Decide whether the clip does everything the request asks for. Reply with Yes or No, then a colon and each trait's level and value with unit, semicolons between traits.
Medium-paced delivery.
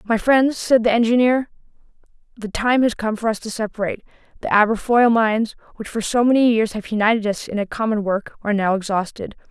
Yes: average, 195 wpm